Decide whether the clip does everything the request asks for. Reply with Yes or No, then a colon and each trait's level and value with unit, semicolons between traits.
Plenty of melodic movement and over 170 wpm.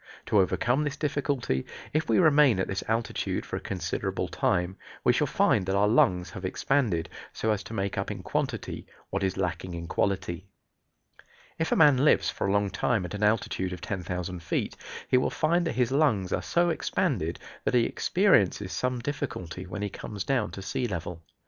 Yes: wide, 6.3 semitones; average, 195 wpm